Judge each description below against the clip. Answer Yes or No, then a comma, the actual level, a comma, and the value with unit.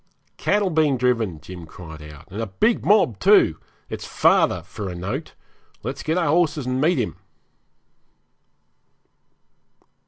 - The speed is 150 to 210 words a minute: No, slow, 135 wpm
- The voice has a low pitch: Yes, low, 125 Hz